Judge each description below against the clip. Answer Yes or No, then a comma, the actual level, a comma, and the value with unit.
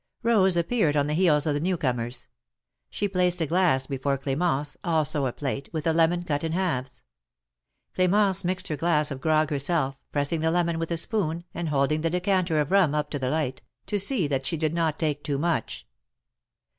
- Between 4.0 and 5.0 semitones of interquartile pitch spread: No, average, 3.5 semitones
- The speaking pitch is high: No, medium, 160 Hz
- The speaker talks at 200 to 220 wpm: Yes, fast, 205 wpm